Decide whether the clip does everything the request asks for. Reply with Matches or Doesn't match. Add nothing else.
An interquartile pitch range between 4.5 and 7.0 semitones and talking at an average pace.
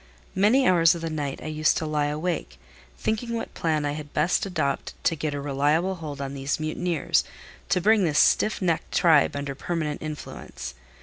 Doesn't match